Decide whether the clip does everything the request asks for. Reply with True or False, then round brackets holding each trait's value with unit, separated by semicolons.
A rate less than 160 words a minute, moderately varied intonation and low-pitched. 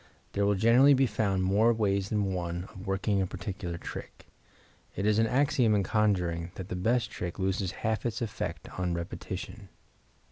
False (175 wpm; 3.1 semitones; 100 Hz)